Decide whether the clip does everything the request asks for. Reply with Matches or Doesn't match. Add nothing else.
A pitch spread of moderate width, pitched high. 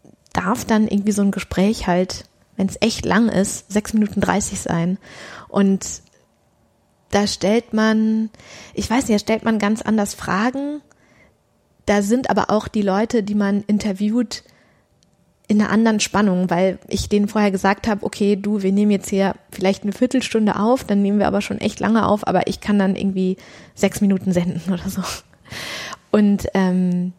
Doesn't match